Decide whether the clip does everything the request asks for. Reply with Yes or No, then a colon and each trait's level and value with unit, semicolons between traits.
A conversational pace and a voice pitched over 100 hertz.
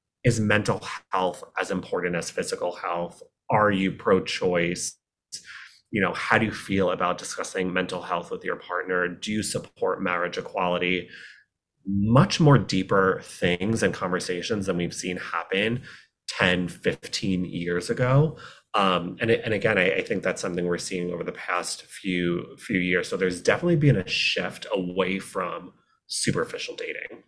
No: average, 155 wpm; very low, 95 Hz